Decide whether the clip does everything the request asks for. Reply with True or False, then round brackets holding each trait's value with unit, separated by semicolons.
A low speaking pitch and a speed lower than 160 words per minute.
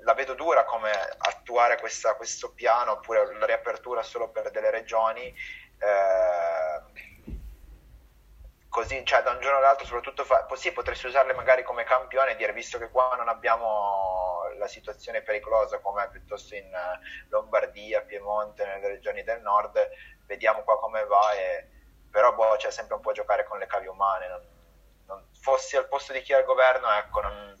False (130 Hz; 170 wpm)